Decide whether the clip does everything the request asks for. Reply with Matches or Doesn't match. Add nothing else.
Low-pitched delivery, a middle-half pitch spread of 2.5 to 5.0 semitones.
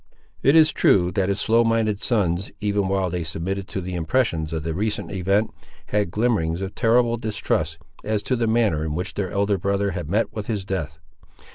Matches